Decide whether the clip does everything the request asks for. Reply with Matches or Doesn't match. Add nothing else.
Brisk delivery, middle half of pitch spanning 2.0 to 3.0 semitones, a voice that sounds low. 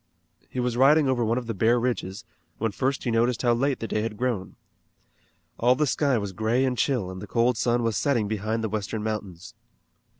Matches